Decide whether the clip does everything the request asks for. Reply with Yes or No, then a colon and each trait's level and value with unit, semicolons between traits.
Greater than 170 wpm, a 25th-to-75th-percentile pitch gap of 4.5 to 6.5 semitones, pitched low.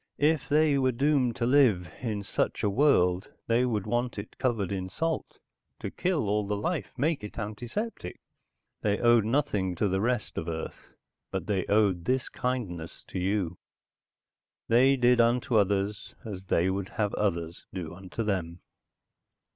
No: average, 160 wpm; average, 4.9 semitones; low, 105 Hz